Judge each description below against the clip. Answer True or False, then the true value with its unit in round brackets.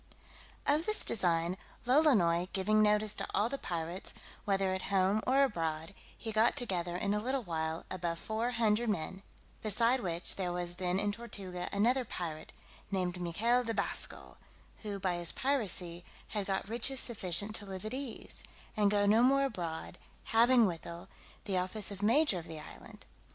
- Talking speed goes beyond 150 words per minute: True (170 wpm)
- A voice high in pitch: True (200 Hz)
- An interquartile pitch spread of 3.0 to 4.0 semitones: False (4.5 semitones)